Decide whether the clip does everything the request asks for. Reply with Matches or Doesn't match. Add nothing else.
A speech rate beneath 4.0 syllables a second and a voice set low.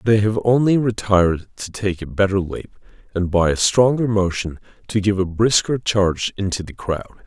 Doesn't match